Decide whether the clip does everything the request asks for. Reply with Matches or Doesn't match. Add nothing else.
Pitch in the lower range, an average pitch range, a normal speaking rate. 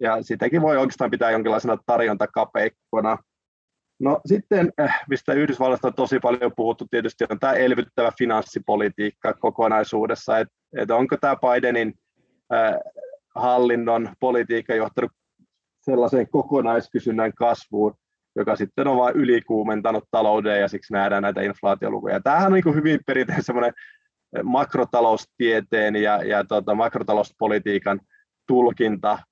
Matches